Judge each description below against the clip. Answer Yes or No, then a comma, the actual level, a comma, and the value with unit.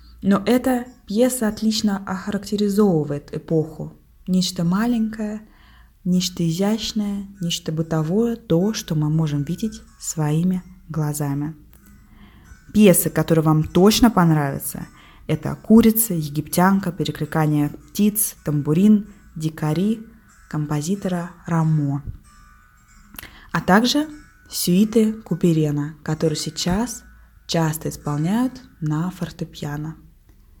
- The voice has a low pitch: No, medium, 175 Hz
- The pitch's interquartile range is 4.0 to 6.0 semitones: Yes, average, 5.3 semitones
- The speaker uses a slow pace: Yes, slow, 85 wpm